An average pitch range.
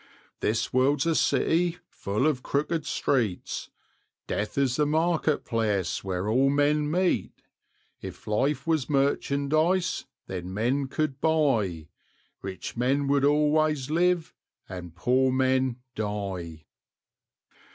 No: wide, 6.1 semitones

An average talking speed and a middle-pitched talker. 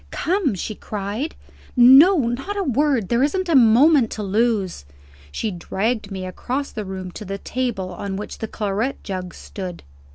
No: average, 165 wpm; high, 220 Hz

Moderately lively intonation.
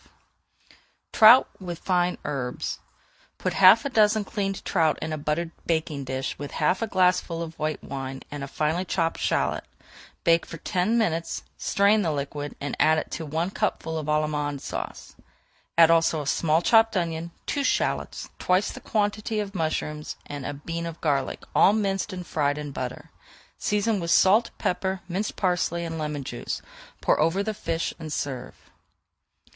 Yes: average, 4.2 semitones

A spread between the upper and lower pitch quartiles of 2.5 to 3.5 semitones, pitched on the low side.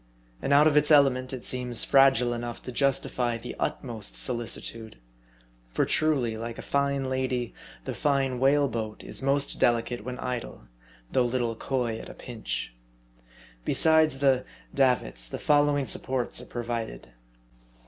Yes: average, 2.8 semitones; low, 125 Hz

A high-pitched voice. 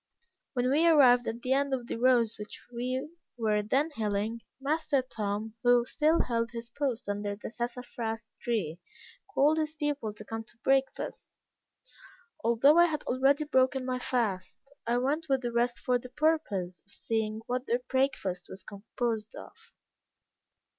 Yes: high, 245 Hz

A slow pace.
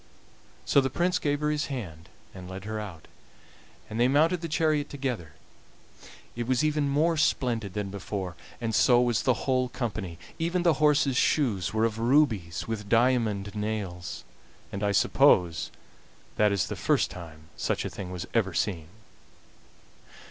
No: average, 160 wpm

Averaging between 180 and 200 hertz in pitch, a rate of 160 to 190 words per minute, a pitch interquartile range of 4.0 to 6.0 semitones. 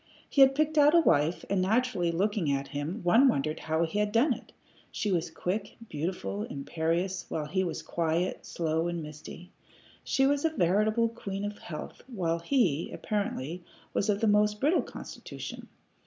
Yes: medium, 185 Hz; average, 170 wpm; average, 5.0 semitones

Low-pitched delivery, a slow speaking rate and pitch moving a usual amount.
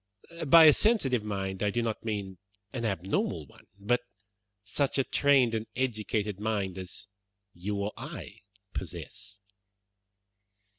Yes: low, 105 Hz; slow, 130 wpm; average, 3.7 semitones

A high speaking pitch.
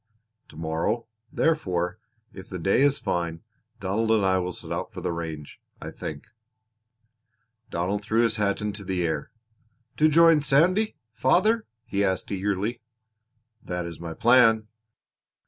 No: low, 100 Hz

